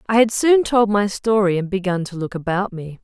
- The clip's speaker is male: No, female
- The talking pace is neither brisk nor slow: No, fast, 240 wpm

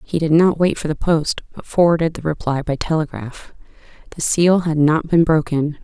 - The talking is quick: No, average, 185 wpm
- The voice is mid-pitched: Yes, medium, 160 Hz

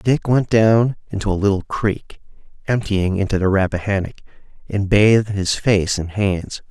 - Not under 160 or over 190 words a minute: No, average, 150 wpm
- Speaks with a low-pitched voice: Yes, low, 100 Hz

